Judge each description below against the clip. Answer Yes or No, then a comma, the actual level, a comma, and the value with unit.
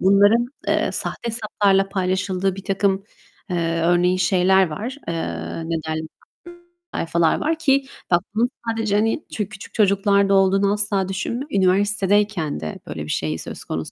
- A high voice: Yes, high, 195 Hz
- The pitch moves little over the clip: No, average, 3.3 semitones